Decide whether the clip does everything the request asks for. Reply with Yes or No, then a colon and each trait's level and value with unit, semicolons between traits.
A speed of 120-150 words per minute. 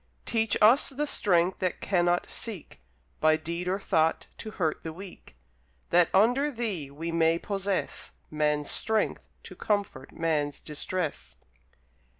Yes: slow, 135 wpm